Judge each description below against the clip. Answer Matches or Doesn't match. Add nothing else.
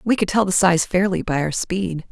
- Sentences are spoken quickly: Matches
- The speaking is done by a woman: Matches